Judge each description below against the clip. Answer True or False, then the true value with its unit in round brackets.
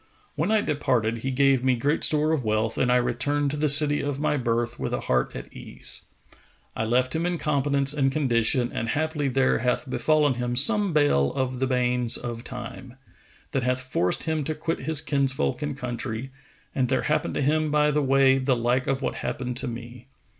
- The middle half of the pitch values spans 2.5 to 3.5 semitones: True (3.2 semitones)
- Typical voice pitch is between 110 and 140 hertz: True (135 Hz)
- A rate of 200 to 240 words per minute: True (205 wpm)